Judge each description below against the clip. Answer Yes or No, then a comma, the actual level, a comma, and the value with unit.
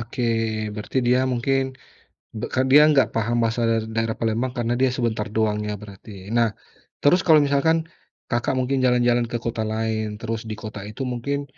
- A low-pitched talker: Yes, low, 120 Hz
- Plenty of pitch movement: No, average, 3.0 semitones